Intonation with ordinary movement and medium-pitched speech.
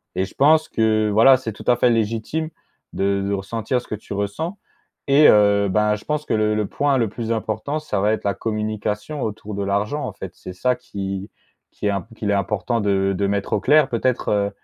No: average, 3.5 semitones; low, 110 Hz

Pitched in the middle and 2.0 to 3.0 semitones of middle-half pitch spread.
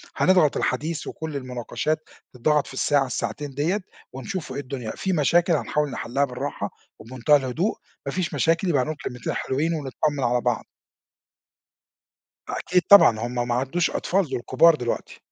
No: medium, 145 Hz; average, 4.5 semitones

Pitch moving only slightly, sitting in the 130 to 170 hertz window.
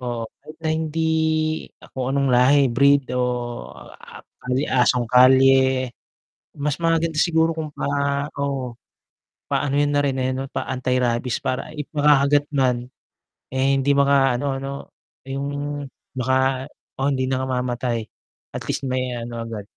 Yes: narrow, 2.0 semitones; low, 135 Hz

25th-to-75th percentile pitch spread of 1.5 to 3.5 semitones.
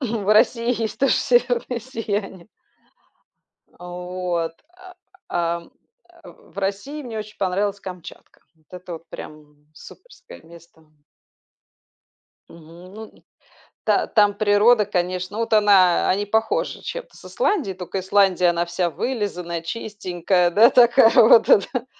No: average, 4.2 semitones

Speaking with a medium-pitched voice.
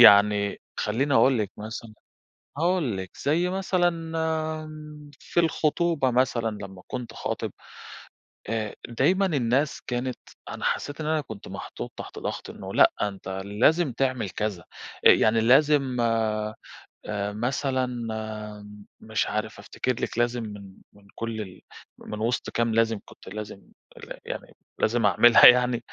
No: low, 120 Hz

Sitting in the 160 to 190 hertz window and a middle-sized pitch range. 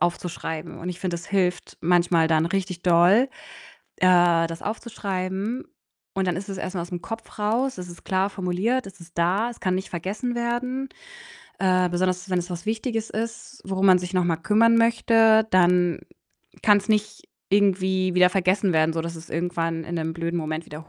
Yes: medium, 185 Hz; average, 3.3 semitones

